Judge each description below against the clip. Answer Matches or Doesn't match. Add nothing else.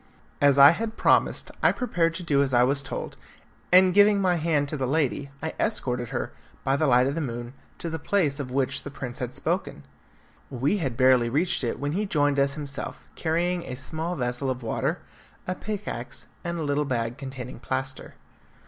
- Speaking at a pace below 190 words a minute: Doesn't match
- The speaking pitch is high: Doesn't match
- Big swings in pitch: Doesn't match